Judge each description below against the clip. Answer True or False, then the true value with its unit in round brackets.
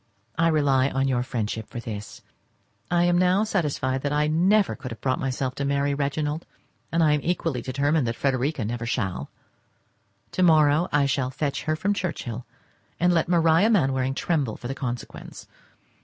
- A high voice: False (140 Hz)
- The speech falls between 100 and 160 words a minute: False (170 wpm)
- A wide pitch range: False (4.2 semitones)